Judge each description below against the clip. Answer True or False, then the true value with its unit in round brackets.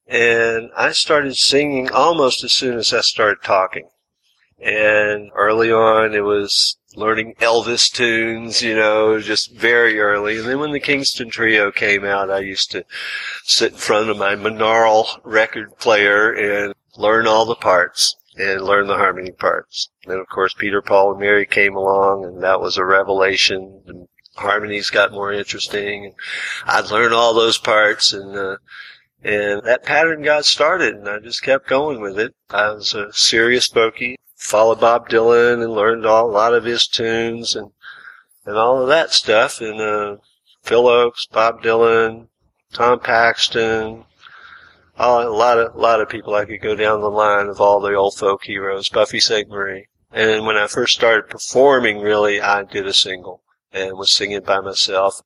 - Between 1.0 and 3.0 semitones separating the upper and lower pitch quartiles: True (2.4 semitones)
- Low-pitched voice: True (110 Hz)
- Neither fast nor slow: True (175 wpm)